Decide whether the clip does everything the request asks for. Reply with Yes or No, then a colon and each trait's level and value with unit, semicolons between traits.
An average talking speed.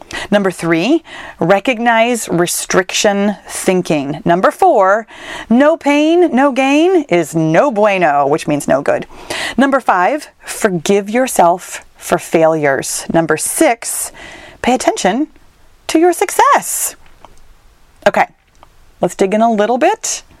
No: slow, 110 wpm